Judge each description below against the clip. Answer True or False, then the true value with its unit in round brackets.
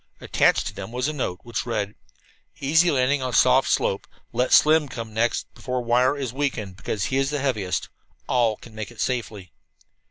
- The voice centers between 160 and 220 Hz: False (125 Hz)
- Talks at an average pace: True (185 wpm)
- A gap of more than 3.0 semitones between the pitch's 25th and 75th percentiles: True (3.5 semitones)